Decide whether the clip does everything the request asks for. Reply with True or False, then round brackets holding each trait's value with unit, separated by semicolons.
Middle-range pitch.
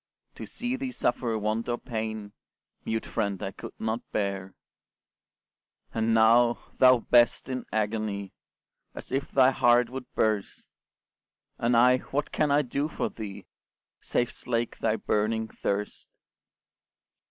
False (115 Hz)